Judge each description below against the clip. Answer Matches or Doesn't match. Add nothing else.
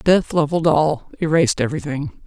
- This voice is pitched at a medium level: Matches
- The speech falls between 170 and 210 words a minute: Doesn't match